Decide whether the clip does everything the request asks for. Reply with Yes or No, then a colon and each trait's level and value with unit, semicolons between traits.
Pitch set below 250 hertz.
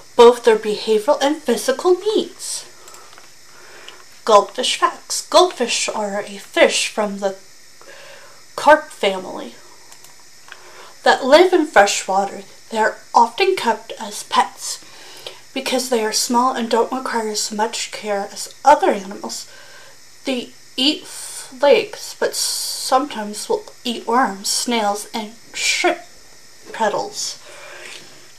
No: very high, 255 Hz